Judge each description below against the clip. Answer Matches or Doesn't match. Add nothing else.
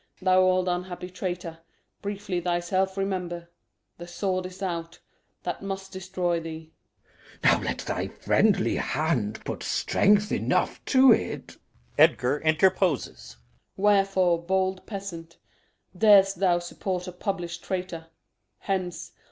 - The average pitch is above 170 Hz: Matches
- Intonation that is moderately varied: Doesn't match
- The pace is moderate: Doesn't match